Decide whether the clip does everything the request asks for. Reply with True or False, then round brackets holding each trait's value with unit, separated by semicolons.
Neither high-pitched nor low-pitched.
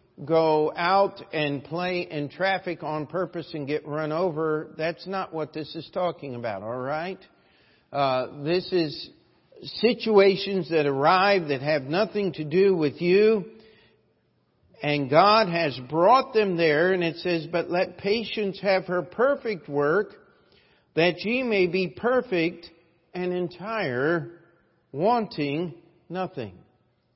True (170 Hz)